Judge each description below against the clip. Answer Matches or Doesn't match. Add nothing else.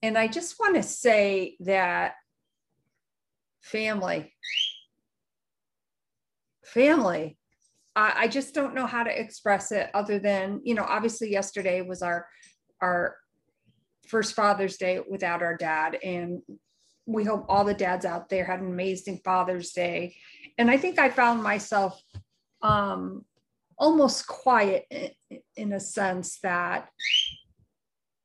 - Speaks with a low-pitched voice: Doesn't match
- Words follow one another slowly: Matches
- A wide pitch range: Doesn't match